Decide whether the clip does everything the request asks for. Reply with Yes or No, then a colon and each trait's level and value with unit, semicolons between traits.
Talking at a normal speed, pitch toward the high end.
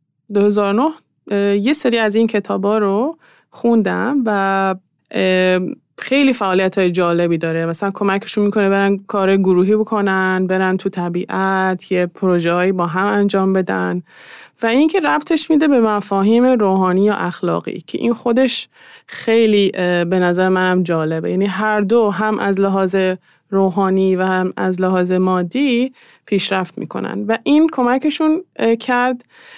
Yes: average, 135 wpm; high, 195 Hz